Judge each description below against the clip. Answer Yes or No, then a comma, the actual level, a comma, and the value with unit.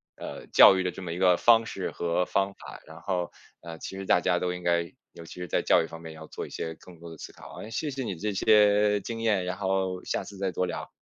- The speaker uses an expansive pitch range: No, average, 2.8 semitones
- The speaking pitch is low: Yes, very low, 90 Hz